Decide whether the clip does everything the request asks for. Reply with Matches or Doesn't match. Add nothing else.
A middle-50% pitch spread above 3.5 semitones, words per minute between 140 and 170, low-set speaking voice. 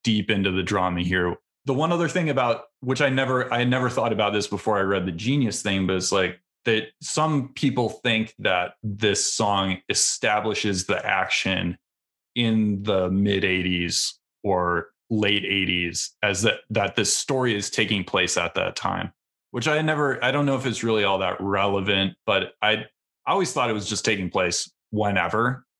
Doesn't match